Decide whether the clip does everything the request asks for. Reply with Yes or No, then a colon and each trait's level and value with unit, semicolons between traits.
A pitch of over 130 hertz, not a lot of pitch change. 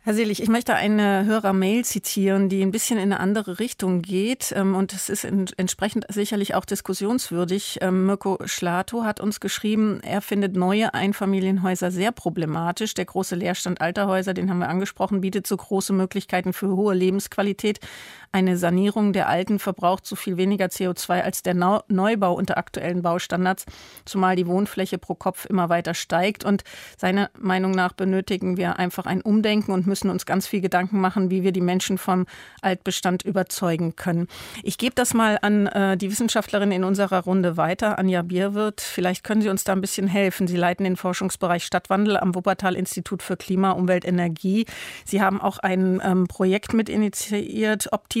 Yes: high, 190 Hz; narrow, 1.7 semitones